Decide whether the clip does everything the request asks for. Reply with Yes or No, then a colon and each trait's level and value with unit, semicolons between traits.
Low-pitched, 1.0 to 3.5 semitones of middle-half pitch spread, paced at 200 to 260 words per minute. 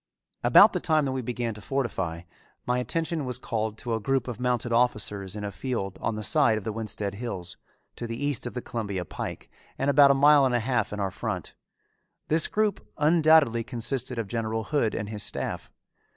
No: low, 120 Hz; average, 4.0 semitones; fast, 205 wpm